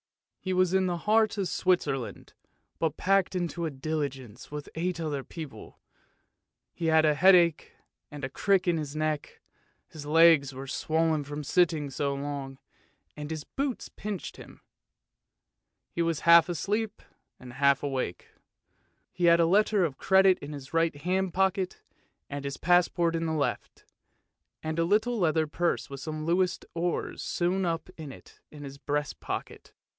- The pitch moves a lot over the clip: No, average, 3.8 semitones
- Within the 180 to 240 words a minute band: No, average, 160 wpm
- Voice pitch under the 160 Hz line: No, medium, 165 Hz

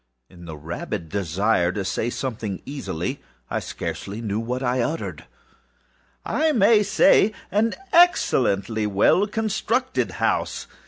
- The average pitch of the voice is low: Yes, low, 115 Hz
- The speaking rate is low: Yes, slow, 130 wpm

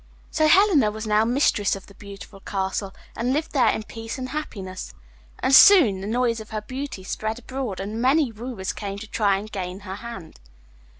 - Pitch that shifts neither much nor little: Yes, average, 4.5 semitones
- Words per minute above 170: Yes, average, 190 wpm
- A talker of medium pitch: No, high, 220 Hz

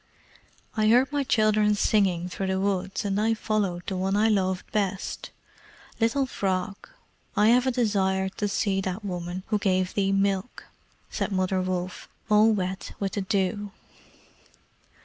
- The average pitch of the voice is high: Yes, high, 195 Hz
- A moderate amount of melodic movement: No, narrow, 2.3 semitones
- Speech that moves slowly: No, average, 150 wpm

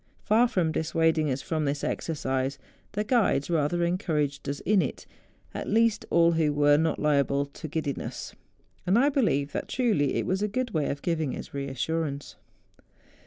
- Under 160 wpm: No, average, 165 wpm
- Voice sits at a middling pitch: Yes, medium, 160 Hz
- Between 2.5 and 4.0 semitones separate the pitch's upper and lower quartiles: No, average, 4.7 semitones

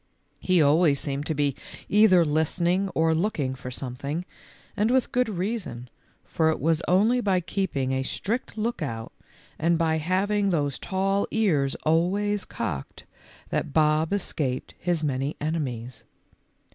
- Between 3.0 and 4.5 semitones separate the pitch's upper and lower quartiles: No, wide, 5.4 semitones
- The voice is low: No, medium, 165 Hz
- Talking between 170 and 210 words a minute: No, slow, 135 wpm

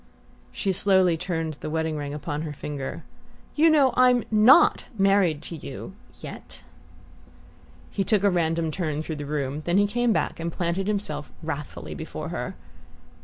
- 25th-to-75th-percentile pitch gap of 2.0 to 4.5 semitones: No, average, 5.0 semitones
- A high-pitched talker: No, medium, 170 Hz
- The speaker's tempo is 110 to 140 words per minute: No, average, 160 wpm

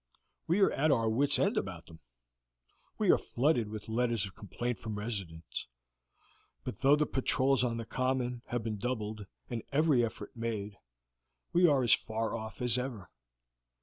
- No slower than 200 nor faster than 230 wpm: No, average, 165 wpm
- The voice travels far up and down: No, average, 3.2 semitones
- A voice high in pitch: No, low, 120 Hz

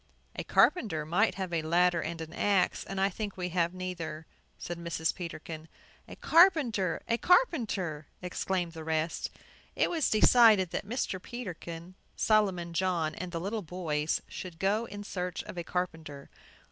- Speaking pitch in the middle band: Yes, medium, 180 Hz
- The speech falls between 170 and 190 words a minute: No, average, 160 wpm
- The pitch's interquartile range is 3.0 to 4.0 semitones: Yes, average, 3.7 semitones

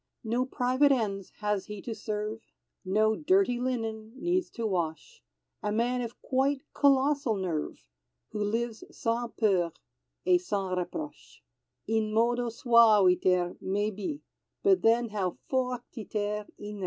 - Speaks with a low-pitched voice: No, high, 225 Hz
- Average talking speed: No, slow, 130 wpm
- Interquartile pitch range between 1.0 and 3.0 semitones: No, average, 3.4 semitones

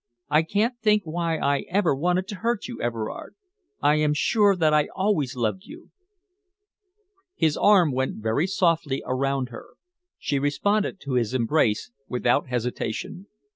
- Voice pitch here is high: No, medium, 155 Hz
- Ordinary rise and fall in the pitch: No, wide, 6.8 semitones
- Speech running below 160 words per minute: Yes, average, 145 wpm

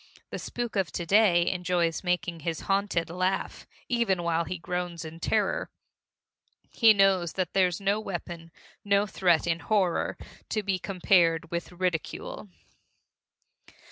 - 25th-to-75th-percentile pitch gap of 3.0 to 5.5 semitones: No, narrow, 2.5 semitones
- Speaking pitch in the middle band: Yes, medium, 180 Hz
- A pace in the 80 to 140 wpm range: Yes, slow, 135 wpm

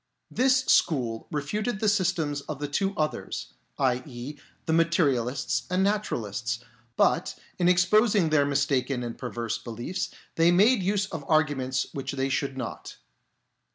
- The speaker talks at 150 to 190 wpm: No, average, 140 wpm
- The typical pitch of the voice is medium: Yes, medium, 145 Hz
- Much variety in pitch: Yes, wide, 6.1 semitones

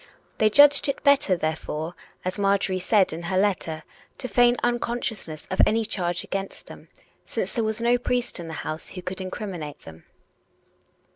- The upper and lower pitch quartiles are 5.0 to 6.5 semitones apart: Yes, wide, 5.4 semitones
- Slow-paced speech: No, average, 165 wpm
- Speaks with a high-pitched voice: Yes, high, 195 Hz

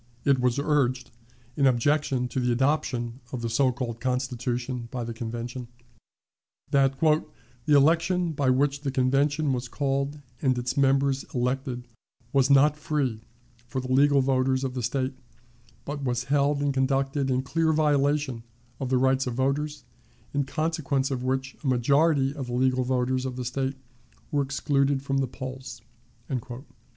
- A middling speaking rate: Yes, average, 155 wpm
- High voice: No, low, 135 Hz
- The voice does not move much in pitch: Yes, narrow, 2.0 semitones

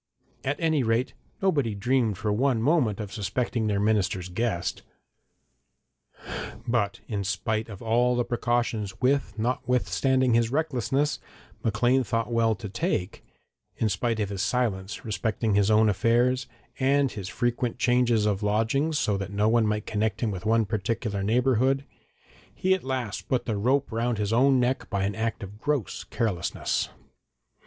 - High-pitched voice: No, low, 115 Hz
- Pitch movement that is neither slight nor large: Yes, average, 3.3 semitones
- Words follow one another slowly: No, average, 155 wpm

